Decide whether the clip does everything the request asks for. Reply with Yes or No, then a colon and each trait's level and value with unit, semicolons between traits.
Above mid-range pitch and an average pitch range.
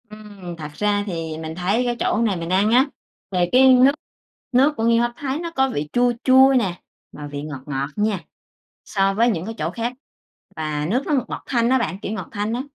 No: high, 210 Hz; wide, 6.0 semitones